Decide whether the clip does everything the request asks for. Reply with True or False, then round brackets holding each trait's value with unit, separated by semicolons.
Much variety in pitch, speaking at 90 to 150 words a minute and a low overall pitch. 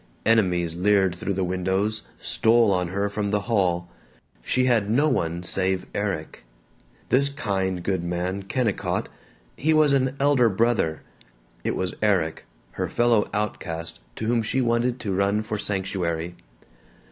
False (4.2 semitones; 145 wpm; 100 Hz)